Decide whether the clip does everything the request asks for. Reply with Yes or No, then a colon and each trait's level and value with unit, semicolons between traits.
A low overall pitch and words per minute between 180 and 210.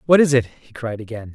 No: low, 125 Hz; fast, 265 wpm